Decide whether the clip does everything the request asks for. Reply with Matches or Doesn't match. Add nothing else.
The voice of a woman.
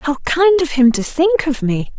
Matches